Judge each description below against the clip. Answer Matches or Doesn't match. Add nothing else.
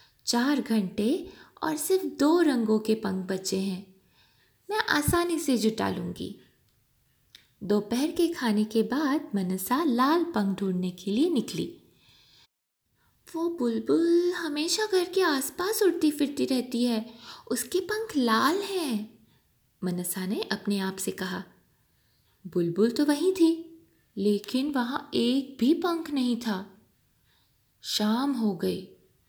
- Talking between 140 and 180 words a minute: Doesn't match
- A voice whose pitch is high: Matches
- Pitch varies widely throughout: Matches